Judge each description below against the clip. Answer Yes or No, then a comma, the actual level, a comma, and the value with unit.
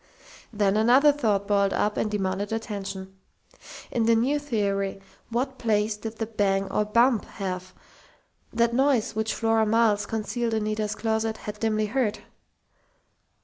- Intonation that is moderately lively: No, narrow, 2.0 semitones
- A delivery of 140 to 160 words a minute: Yes, average, 145 wpm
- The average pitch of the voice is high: Yes, high, 220 Hz